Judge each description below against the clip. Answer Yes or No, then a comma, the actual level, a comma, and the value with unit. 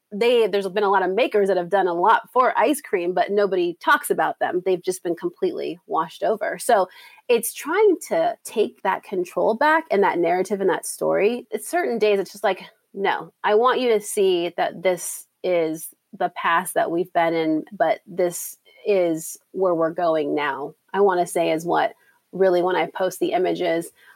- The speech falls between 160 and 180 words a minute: No, average, 200 wpm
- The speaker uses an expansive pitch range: Yes, wide, 6.1 semitones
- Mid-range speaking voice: No, high, 200 Hz